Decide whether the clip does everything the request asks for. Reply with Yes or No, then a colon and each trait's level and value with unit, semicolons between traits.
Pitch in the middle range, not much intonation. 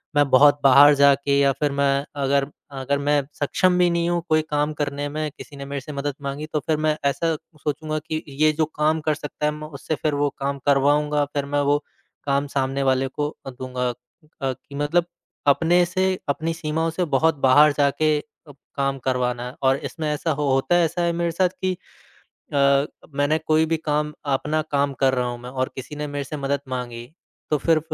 Yes: medium, 145 Hz; narrow, 2.0 semitones